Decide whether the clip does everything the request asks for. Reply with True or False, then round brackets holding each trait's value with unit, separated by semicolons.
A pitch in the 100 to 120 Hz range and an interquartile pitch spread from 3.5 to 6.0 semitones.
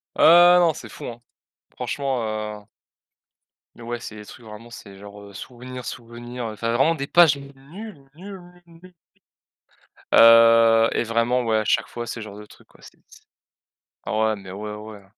True (115 Hz; 3.8 semitones)